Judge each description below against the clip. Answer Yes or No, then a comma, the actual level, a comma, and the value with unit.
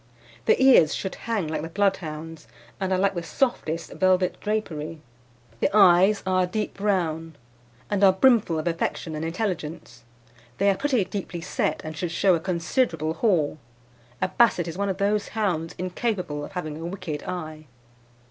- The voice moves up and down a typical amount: Yes, average, 3.6 semitones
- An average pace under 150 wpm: No, average, 165 wpm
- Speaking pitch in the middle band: Yes, medium, 180 Hz